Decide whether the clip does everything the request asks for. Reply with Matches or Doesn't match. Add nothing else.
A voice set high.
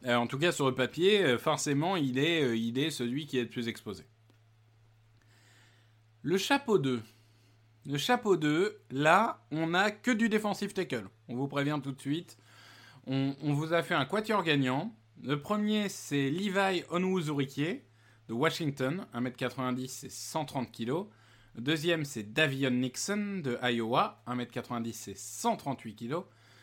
Doesn't match